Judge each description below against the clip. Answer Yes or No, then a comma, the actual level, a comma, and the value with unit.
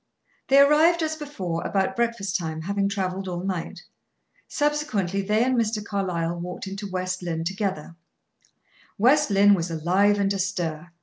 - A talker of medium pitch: No, high, 195 Hz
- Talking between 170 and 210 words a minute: No, average, 145 wpm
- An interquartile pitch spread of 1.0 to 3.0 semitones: No, average, 4.1 semitones